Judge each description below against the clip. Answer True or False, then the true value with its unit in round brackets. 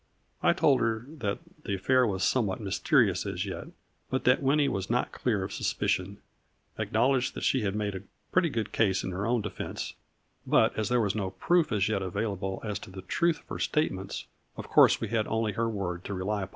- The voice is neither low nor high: False (105 Hz)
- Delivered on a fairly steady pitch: False (4.1 semitones)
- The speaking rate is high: True (215 wpm)